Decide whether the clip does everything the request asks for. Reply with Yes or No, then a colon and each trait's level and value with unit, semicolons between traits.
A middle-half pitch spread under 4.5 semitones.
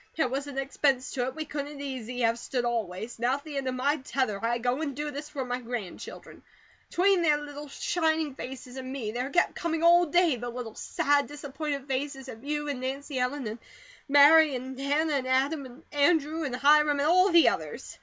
Yes: average, 2.9 semitones